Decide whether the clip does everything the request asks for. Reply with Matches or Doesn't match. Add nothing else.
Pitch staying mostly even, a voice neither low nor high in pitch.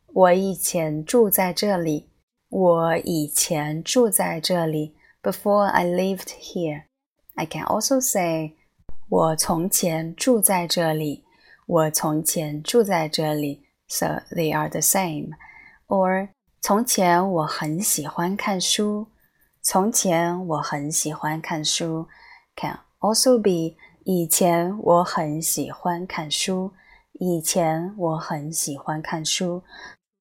Doesn't match